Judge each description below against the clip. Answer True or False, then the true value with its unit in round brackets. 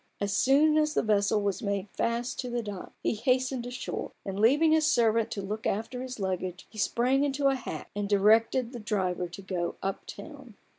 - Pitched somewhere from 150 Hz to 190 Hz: False (225 Hz)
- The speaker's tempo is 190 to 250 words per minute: True (200 wpm)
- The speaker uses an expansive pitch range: False (4.3 semitones)